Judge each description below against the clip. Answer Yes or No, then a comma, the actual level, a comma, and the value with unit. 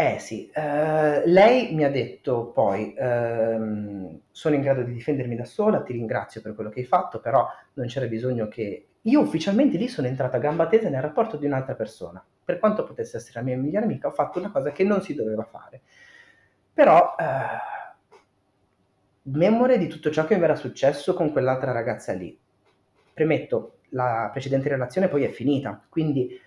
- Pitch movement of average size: No, wide, 5.7 semitones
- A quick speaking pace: Yes, fast, 180 wpm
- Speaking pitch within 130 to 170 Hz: Yes, medium, 140 Hz